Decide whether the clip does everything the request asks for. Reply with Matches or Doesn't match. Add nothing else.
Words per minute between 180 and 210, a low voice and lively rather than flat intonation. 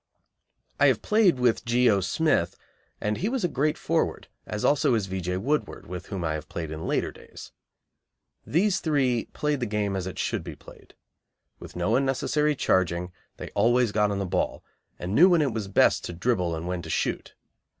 Matches